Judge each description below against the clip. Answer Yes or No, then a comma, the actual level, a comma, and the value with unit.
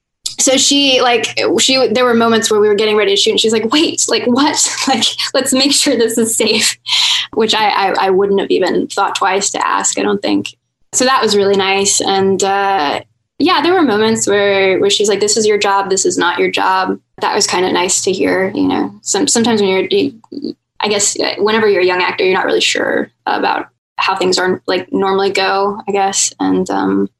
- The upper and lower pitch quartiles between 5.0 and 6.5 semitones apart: Yes, average, 5.3 semitones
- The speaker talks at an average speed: No, fast, 225 wpm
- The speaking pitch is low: No, high, 215 Hz